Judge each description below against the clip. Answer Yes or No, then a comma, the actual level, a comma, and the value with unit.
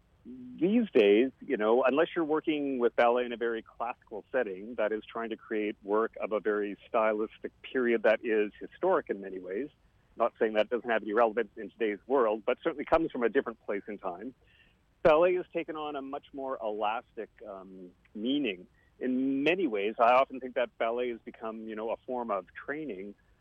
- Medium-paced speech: Yes, average, 195 wpm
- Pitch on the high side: No, low, 120 Hz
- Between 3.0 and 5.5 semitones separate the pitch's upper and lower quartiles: Yes, average, 4.8 semitones